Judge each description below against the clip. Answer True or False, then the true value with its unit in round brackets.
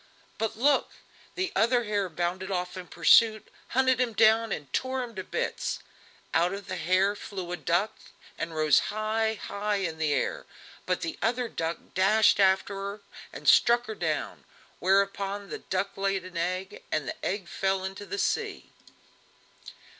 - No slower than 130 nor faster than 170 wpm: True (165 wpm)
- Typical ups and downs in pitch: True (3.3 semitones)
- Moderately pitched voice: False (195 Hz)